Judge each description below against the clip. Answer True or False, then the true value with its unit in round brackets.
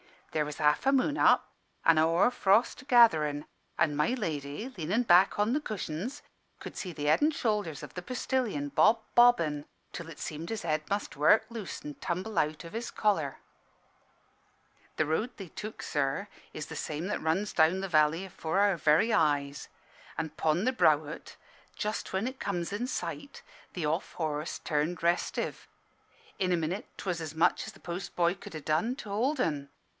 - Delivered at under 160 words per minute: False (190 wpm)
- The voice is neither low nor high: True (170 Hz)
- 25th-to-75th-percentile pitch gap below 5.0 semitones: False (5.6 semitones)